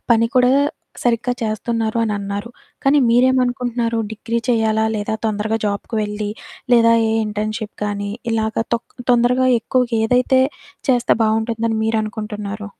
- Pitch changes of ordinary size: No, narrow, 2.0 semitones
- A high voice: Yes, high, 225 Hz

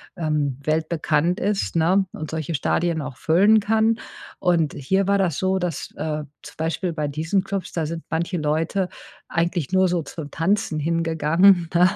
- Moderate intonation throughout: Yes, average, 3.2 semitones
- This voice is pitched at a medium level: Yes, medium, 170 Hz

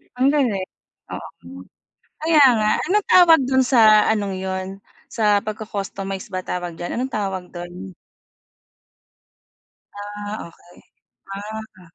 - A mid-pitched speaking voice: No, high, 205 Hz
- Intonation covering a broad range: No, average, 3.6 semitones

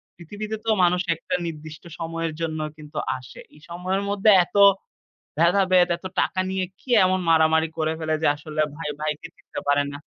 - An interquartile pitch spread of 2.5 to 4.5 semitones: Yes, average, 2.9 semitones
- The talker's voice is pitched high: No, medium, 165 Hz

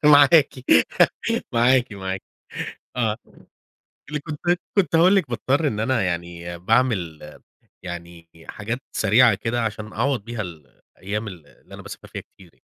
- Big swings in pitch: Yes, wide, 6.3 semitones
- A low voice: Yes, low, 110 Hz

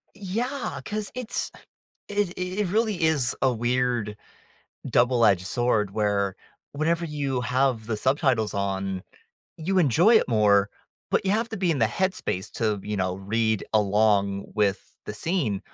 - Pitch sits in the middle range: No, low, 120 Hz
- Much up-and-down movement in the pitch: Yes, wide, 8.8 semitones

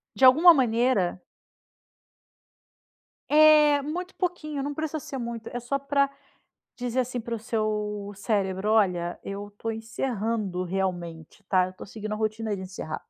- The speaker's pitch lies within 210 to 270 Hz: Yes, high, 225 Hz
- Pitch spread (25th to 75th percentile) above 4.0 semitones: Yes, wide, 5.6 semitones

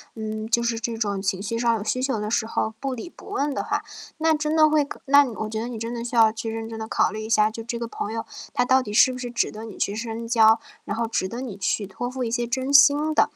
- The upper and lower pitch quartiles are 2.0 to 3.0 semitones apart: Yes, average, 2.7 semitones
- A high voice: Yes, high, 230 Hz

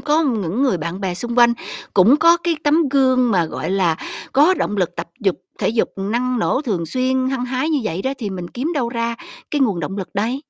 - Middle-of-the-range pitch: No, high, 240 Hz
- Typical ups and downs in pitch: No, wide, 5.7 semitones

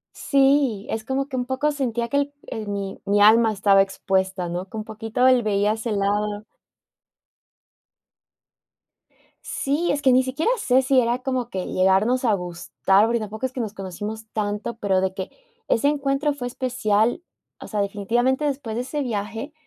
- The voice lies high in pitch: Yes, high, 225 Hz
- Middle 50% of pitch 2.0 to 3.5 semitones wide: No, average, 4.3 semitones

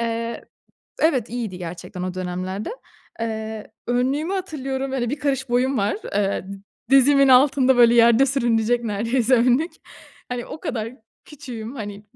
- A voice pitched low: No, high, 240 Hz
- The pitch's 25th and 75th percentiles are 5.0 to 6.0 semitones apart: No, average, 3.5 semitones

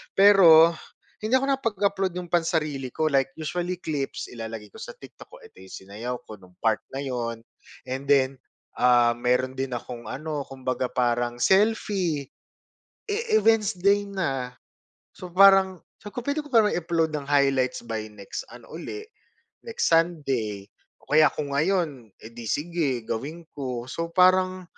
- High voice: No, medium, 150 Hz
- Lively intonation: Yes, wide, 6.9 semitones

